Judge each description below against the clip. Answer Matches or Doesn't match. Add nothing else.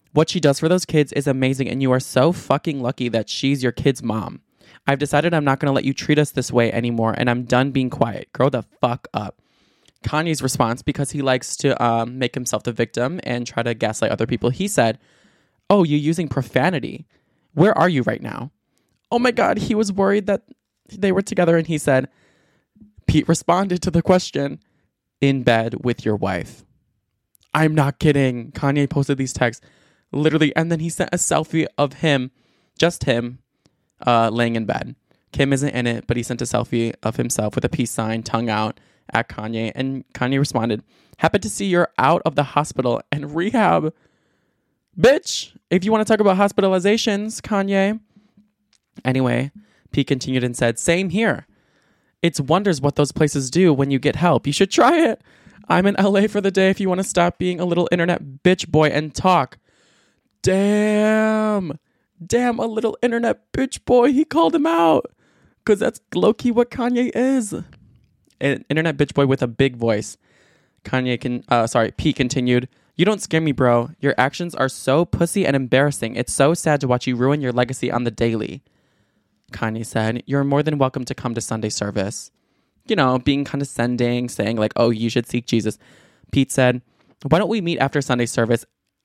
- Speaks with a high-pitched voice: Doesn't match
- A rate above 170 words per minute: Matches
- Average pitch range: Doesn't match